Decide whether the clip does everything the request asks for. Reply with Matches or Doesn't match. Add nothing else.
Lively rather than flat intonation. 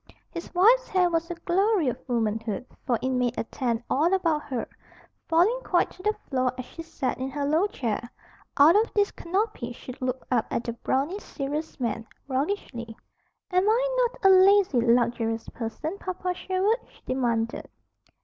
Matches